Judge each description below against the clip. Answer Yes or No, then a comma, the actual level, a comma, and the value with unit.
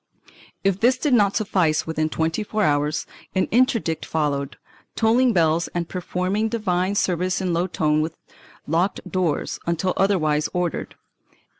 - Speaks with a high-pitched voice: No, medium, 180 Hz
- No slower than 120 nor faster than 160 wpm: Yes, average, 140 wpm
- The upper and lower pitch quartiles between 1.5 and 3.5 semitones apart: No, average, 4.1 semitones